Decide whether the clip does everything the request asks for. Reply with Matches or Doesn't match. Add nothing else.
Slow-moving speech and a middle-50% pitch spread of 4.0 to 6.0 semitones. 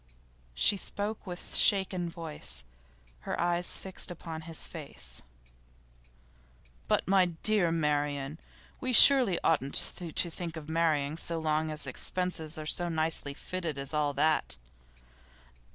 Doesn't match